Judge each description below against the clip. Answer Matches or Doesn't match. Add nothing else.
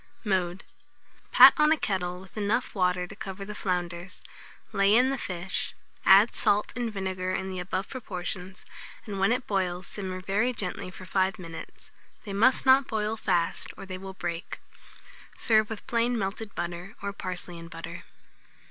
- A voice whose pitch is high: Matches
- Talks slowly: Doesn't match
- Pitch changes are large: Doesn't match